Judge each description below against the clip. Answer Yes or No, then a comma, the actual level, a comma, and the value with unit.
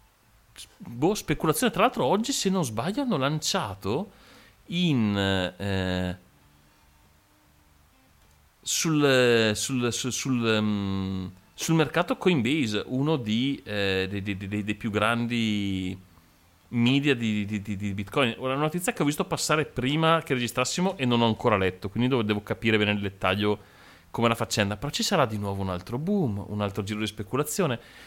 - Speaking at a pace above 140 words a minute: Yes, average, 155 wpm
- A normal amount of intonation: No, wide, 6.0 semitones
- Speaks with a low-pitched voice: Yes, low, 110 Hz